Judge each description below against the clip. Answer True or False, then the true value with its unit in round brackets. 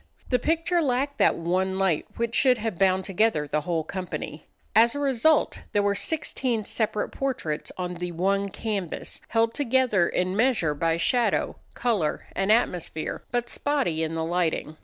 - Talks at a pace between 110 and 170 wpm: True (160 wpm)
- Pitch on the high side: True (200 Hz)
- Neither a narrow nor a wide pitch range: False (6.0 semitones)